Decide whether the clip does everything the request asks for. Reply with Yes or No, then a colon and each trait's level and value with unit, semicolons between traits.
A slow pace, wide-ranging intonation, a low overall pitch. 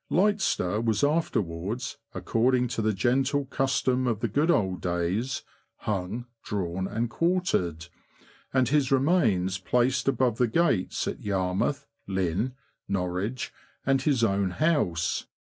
Yes: slow, 125 wpm; wide, 6.0 semitones; low, 115 Hz